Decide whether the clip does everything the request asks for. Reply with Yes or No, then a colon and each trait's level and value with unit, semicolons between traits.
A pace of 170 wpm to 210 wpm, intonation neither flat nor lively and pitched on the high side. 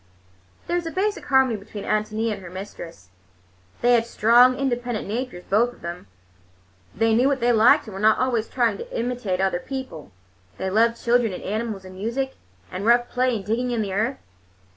Yes: average, 190 wpm; average, 3.5 semitones; high, 230 Hz